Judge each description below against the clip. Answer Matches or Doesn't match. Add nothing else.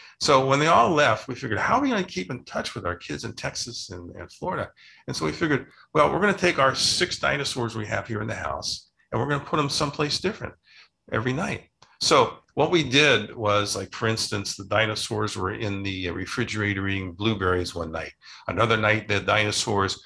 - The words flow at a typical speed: Doesn't match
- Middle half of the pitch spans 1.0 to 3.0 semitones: Doesn't match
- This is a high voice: Doesn't match